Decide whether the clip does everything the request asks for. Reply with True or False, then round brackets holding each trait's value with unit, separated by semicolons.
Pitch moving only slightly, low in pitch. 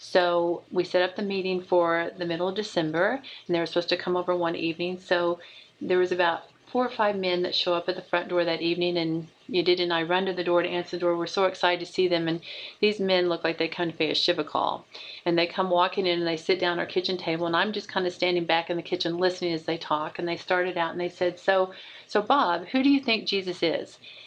False (1.4 semitones; 175 Hz)